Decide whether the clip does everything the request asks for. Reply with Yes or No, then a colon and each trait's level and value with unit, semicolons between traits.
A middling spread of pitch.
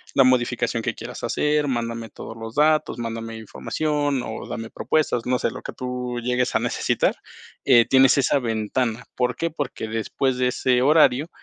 Yes: average, 3.0 semitones